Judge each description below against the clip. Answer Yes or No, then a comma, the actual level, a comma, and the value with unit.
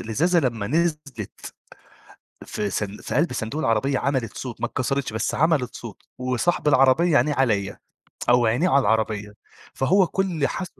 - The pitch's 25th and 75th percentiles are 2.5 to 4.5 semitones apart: No, wide, 5.4 semitones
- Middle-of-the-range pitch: No, low, 130 Hz